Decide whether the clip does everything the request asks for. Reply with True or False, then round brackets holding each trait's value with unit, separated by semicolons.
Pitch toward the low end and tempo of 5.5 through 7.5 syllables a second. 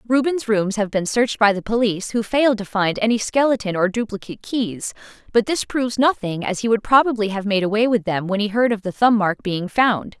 False (220 Hz; 5.7 syllables/s)